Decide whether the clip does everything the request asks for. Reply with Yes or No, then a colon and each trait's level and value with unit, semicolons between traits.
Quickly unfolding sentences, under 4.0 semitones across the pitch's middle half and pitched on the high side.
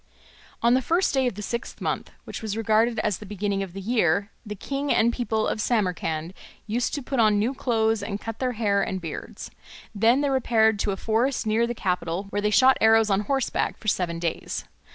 Yes: fast, 215 wpm; average, 3.1 semitones; high, 220 Hz